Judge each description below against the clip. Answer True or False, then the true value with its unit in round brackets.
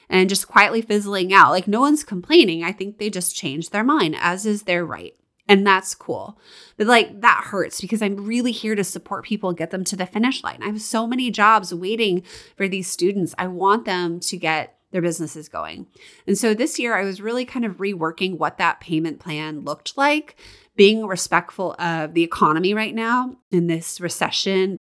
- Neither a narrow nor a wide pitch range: True (3.8 semitones)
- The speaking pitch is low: False (195 Hz)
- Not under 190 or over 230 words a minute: True (200 wpm)